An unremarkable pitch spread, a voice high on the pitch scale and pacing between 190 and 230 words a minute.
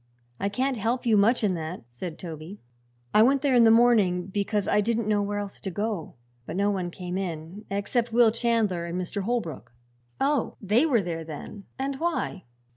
Yes: average, 4.4 semitones; high, 205 Hz; average, 195 wpm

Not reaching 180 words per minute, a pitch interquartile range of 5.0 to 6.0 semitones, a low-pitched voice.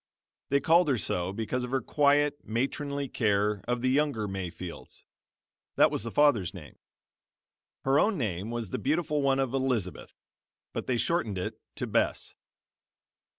Yes: average, 150 wpm; wide, 5.5 semitones; low, 125 Hz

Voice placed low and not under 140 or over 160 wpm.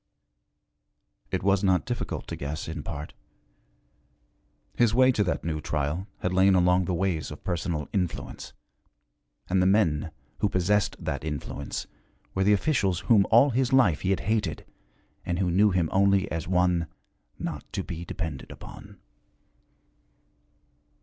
Yes: very low, 90 Hz; average, 145 wpm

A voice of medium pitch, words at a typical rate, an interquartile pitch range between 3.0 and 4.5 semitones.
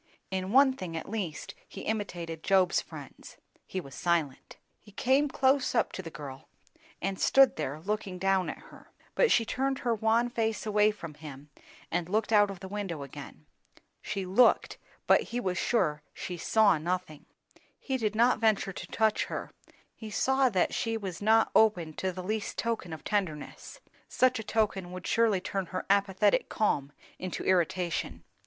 No: high, 195 Hz; average, 175 wpm; average, 4.1 semitones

